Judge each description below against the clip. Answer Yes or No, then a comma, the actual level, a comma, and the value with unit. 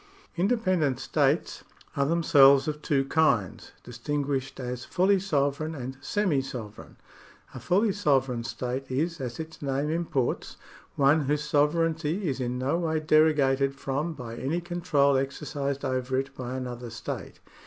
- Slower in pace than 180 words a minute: Yes, average, 145 wpm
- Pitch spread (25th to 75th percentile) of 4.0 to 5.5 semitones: No, average, 3.3 semitones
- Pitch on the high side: No, medium, 140 Hz